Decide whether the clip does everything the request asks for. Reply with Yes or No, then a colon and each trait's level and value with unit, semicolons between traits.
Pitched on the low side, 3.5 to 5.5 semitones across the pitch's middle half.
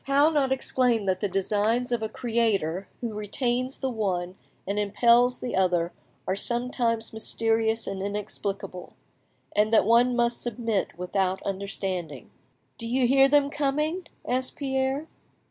No: high, 230 Hz; average, 4.3 semitones